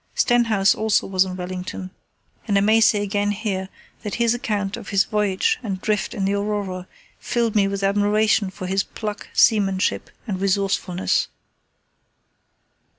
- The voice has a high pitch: Yes, high, 200 Hz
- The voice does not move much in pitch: Yes, narrow, 1.8 semitones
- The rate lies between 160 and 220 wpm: No, average, 150 wpm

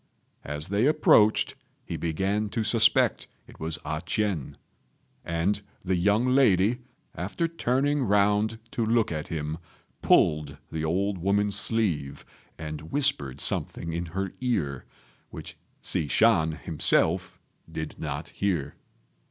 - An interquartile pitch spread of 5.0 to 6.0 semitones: Yes, wide, 5.5 semitones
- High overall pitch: No, very low, 95 Hz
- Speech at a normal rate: No, slow, 125 wpm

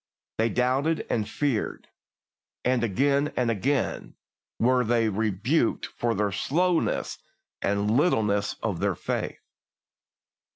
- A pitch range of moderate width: Yes, average, 4.7 semitones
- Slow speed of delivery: Yes, slow, 110 wpm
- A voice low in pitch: Yes, low, 120 Hz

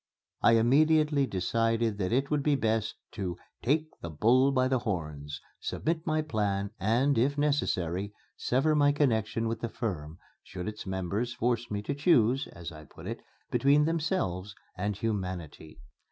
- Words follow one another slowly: No, average, 155 wpm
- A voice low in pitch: Yes, low, 115 Hz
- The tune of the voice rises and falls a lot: Yes, wide, 6.5 semitones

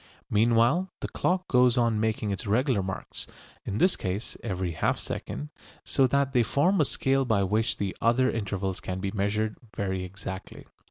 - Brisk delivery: No, average, 170 wpm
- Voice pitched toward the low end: Yes, low, 110 Hz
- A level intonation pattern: No, average, 4.7 semitones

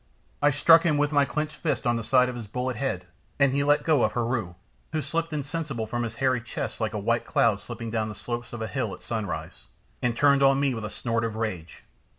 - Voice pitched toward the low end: Yes, low, 125 Hz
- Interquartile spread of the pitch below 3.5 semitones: No, average, 4.1 semitones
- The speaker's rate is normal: No, fast, 240 wpm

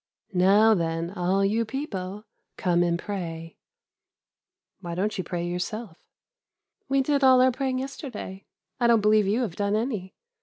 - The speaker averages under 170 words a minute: Yes, average, 150 wpm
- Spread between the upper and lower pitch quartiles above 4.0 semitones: Yes, average, 4.9 semitones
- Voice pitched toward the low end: No, high, 205 Hz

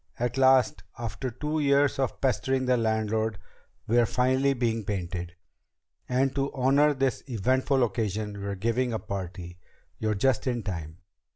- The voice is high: No, low, 120 Hz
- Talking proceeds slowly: No, average, 145 wpm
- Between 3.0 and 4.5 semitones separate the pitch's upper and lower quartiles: Yes, average, 4.1 semitones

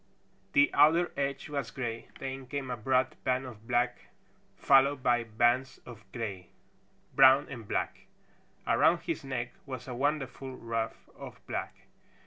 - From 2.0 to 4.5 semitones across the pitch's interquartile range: Yes, narrow, 2.4 semitones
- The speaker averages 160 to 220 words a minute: No, average, 140 wpm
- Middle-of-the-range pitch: No, low, 130 Hz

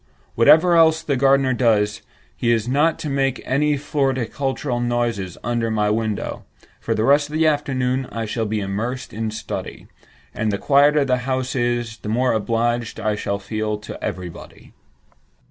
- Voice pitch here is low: Yes, low, 120 Hz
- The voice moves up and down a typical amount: Yes, average, 3.9 semitones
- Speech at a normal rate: Yes, average, 160 wpm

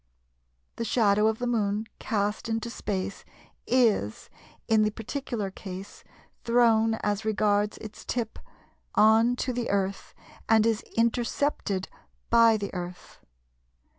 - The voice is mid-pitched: No, high, 220 Hz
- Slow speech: Yes, slow, 120 wpm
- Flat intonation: Yes, narrow, 2.3 semitones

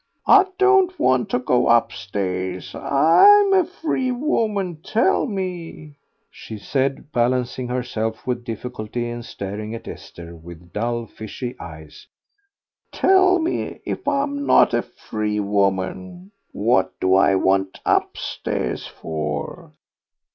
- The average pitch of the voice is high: No, low, 120 Hz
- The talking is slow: Yes, slow, 120 wpm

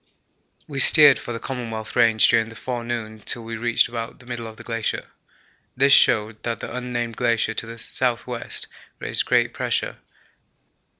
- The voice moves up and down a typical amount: No, narrow, 1.4 semitones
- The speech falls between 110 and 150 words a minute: No, average, 165 wpm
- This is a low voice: Yes, low, 115 Hz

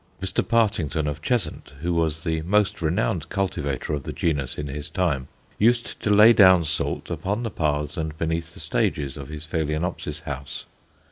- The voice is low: Yes, very low, 80 Hz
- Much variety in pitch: No, average, 4.1 semitones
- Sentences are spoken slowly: No, average, 175 wpm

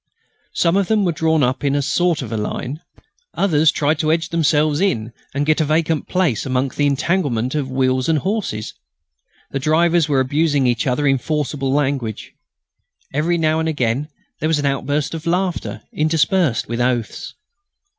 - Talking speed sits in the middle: Yes, average, 175 wpm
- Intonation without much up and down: No, average, 3.5 semitones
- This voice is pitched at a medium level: Yes, medium, 150 Hz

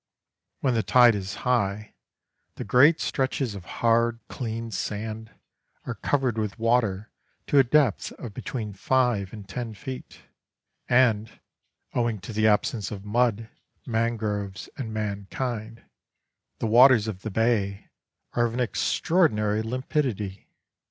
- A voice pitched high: No, low, 115 Hz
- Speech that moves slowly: Yes, slow, 130 wpm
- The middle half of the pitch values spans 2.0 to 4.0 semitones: Yes, average, 3.0 semitones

